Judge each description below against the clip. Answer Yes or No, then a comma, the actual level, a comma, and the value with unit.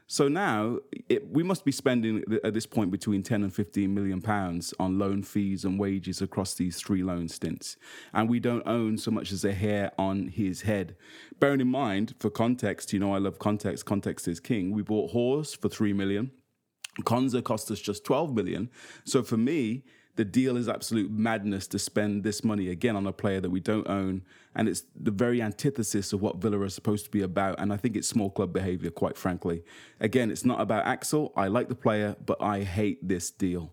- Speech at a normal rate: No, fast, 210 wpm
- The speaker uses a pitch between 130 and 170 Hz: No, low, 105 Hz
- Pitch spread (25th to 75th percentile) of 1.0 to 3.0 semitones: Yes, narrow, 2.5 semitones